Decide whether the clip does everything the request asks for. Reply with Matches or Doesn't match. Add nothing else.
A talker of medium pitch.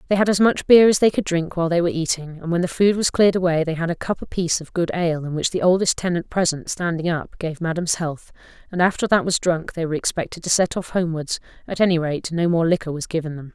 Matches